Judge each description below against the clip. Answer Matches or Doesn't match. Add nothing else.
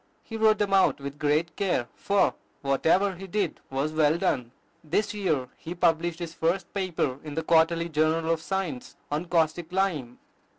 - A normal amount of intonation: Matches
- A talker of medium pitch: Matches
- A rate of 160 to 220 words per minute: Matches